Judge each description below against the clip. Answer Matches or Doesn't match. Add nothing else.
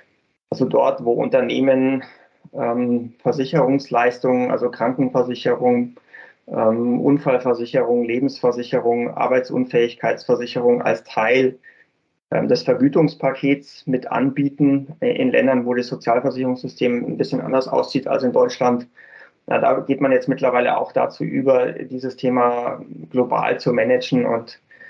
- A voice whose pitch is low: Matches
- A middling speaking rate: Doesn't match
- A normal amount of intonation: Doesn't match